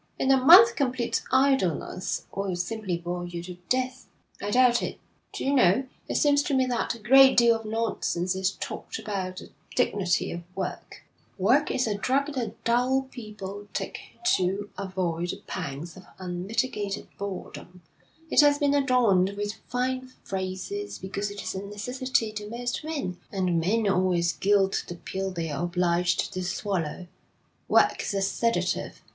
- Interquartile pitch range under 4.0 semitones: No, wide, 5.5 semitones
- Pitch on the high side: Yes, high, 205 Hz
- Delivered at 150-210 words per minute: Yes, average, 160 wpm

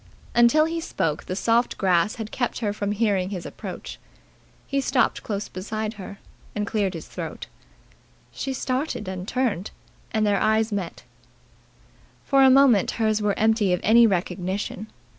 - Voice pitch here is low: No, high, 215 Hz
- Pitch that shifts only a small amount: No, average, 3.5 semitones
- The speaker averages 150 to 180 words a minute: Yes, average, 155 wpm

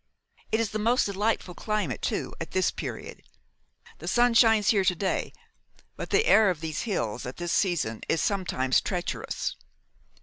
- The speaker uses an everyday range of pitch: Yes, average, 4.6 semitones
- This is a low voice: No, high, 190 Hz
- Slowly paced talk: No, average, 165 wpm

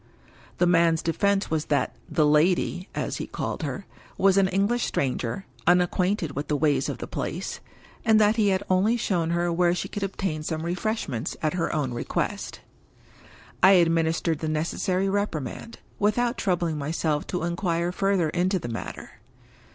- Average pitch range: Yes, average, 3.7 semitones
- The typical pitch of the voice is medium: Yes, medium, 175 Hz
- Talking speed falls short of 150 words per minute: No, average, 160 wpm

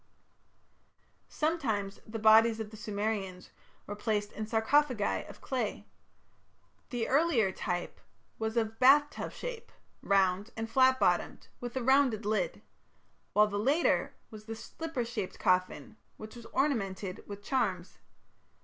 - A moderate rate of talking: No, slow, 130 wpm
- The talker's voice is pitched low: No, high, 220 Hz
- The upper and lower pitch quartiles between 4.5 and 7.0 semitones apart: No, average, 4.0 semitones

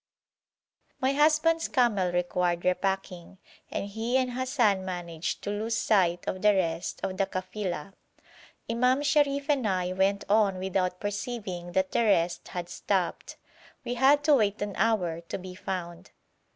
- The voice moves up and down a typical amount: Yes, average, 4.7 semitones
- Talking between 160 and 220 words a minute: No, average, 150 wpm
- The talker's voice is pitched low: No, high, 195 Hz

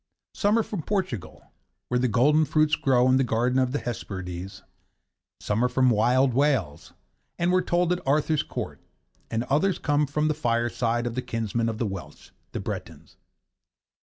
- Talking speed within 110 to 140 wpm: No, average, 175 wpm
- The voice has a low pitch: Yes, low, 130 Hz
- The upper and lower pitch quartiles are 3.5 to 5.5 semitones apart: Yes, average, 4.7 semitones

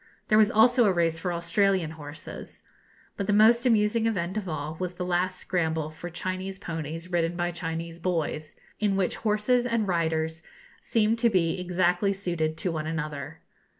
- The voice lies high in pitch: No, medium, 180 Hz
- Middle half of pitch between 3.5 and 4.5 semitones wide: Yes, average, 3.9 semitones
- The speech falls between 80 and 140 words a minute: No, average, 170 wpm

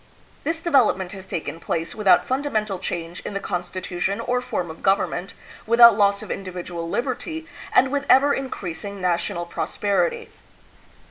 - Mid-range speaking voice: No, high, 200 Hz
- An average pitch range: No, wide, 6.1 semitones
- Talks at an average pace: Yes, average, 145 wpm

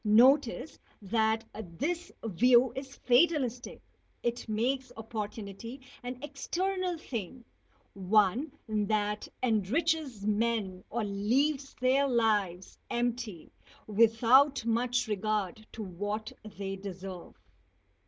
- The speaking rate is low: Yes, slow, 95 wpm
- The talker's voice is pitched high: Yes, high, 225 Hz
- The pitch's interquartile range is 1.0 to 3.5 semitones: No, average, 3.9 semitones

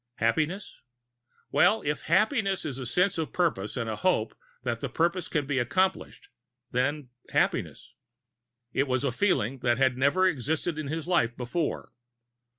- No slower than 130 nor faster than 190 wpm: Yes, average, 155 wpm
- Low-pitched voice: No, medium, 145 Hz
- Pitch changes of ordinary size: No, wide, 6.0 semitones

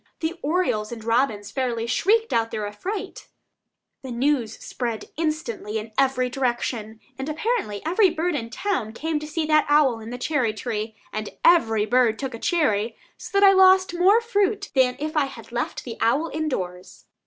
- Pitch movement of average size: No, wide, 6.4 semitones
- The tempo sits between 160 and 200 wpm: Yes, average, 180 wpm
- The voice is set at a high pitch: Yes, very high, 265 Hz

